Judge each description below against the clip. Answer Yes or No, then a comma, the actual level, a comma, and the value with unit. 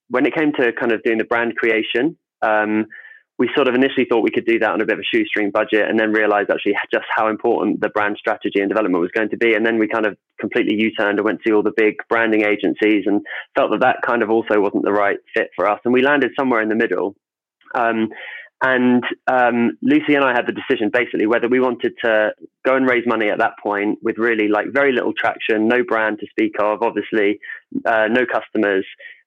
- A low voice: Yes, low, 115 Hz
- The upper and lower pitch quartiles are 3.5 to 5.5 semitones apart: No, average, 2.9 semitones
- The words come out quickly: Yes, fast, 235 wpm